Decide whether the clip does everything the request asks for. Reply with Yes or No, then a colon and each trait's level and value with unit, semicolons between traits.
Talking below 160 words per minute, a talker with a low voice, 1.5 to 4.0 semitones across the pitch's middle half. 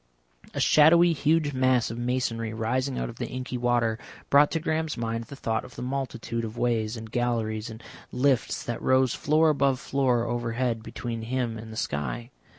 No: average, 180 wpm; low, 120 Hz; average, 2.7 semitones